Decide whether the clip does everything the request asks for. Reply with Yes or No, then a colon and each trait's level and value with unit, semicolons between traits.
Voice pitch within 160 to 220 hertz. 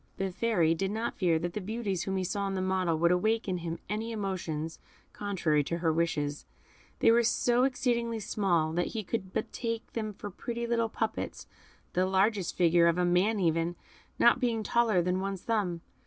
Yes: high, 190 Hz